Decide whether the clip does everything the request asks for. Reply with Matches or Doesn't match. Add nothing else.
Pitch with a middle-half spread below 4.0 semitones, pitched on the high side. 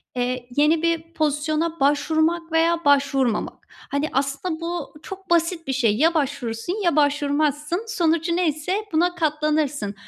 Matches